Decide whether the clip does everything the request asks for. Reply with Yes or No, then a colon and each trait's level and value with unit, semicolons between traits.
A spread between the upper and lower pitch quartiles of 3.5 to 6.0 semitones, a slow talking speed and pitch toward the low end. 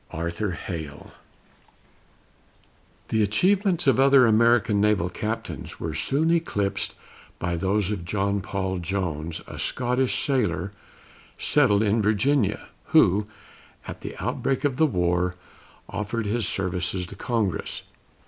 Yes: average, 5.0 semitones; slow, 120 wpm; low, 105 Hz